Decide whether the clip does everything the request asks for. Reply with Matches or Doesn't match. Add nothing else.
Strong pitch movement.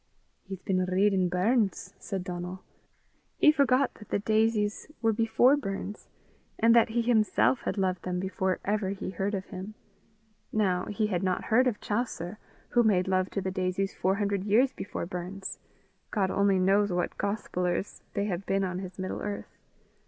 Doesn't match